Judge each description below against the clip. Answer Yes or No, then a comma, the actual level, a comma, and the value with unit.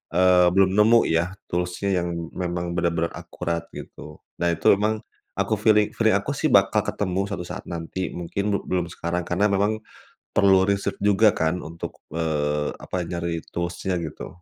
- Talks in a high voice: No, very low, 90 Hz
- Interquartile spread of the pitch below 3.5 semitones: Yes, average, 2.7 semitones